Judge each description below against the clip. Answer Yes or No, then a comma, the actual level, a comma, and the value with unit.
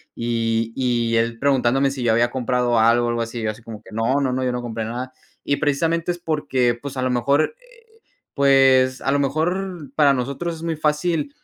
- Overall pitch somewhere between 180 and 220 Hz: No, low, 130 Hz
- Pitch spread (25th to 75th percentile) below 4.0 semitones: Yes, average, 3.5 semitones